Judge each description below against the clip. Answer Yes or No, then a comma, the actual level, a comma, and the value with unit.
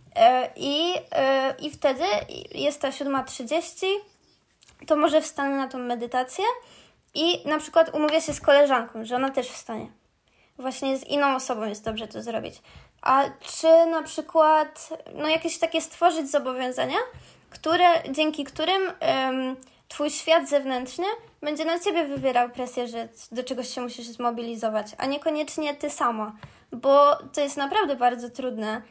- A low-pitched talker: No, very high, 285 Hz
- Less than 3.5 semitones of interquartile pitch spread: No, average, 4.0 semitones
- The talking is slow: No, average, 145 wpm